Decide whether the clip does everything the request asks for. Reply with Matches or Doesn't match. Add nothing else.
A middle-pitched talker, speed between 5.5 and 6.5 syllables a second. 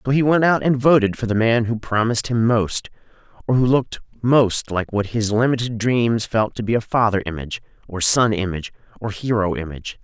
Doesn't match